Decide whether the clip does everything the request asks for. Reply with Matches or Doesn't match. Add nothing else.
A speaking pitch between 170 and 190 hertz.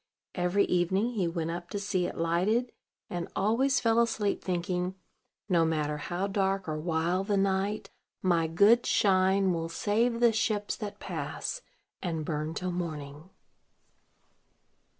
Matches